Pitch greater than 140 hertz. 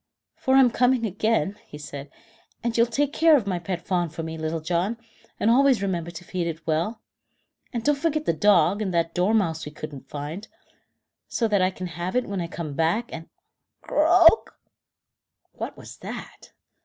Yes: high, 190 Hz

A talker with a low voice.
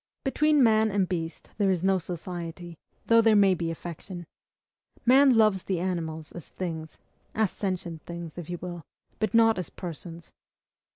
No: medium, 180 Hz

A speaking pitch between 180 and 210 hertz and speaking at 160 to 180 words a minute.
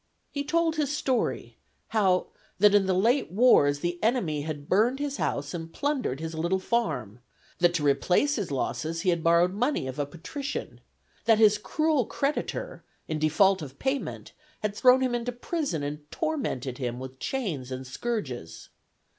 Yes: high, 190 Hz; average, 165 wpm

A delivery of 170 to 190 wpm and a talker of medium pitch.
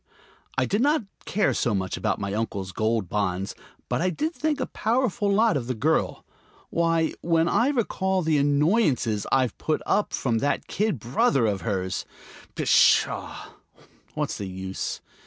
No: average, 160 wpm; medium, 145 Hz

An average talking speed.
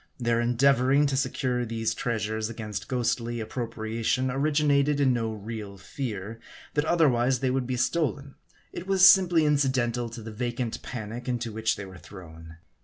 Yes: average, 165 wpm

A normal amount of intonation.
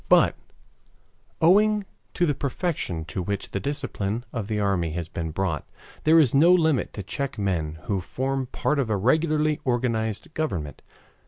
No: wide, 7.9 semitones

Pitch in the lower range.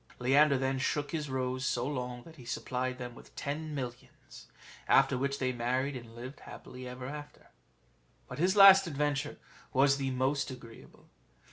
Yes: low, 130 Hz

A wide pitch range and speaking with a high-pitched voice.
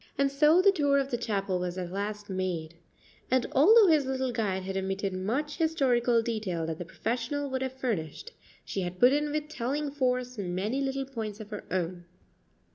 Yes: wide, 6.4 semitones; high, 240 Hz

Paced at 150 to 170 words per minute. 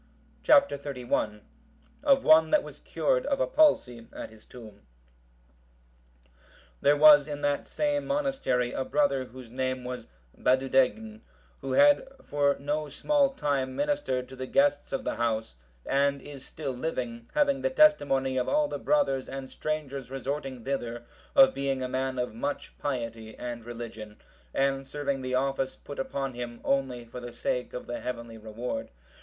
Yes: average, 160 wpm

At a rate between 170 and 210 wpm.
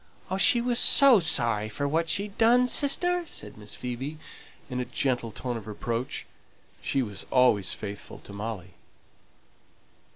No: average, 140 wpm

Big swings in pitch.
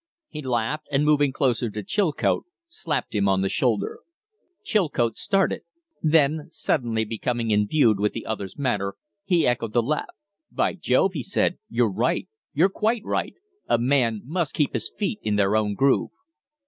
Yes: wide, 5.8 semitones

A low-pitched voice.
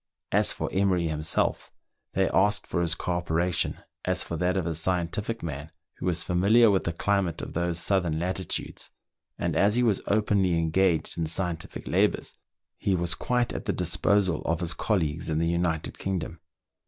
Yes: very low, 90 Hz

